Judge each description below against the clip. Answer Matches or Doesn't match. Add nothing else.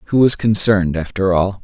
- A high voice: Doesn't match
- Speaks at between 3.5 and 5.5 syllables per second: Matches